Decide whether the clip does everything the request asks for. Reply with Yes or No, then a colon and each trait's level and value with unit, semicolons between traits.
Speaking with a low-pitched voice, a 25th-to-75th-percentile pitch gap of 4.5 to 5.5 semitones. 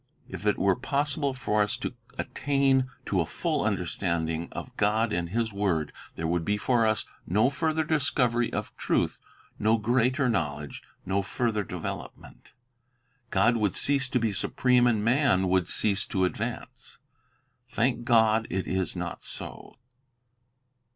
Yes: low, 110 Hz; average, 4.8 semitones